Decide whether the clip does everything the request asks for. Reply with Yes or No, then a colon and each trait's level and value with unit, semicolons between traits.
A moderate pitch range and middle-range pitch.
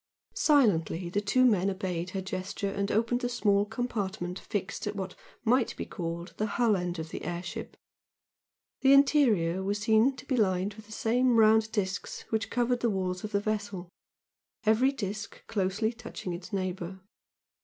No: average, 3.4 semitones; high, 205 Hz